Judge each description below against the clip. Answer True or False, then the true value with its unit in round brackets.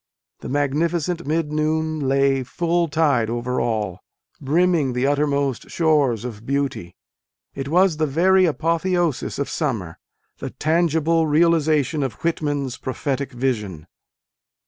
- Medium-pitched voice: True (145 Hz)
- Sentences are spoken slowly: True (125 wpm)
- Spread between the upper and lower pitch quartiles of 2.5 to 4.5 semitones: True (3.8 semitones)